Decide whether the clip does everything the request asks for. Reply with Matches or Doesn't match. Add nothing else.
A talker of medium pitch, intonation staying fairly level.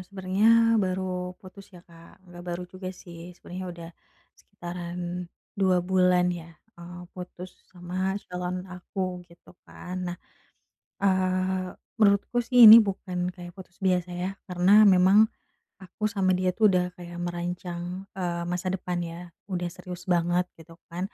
Matches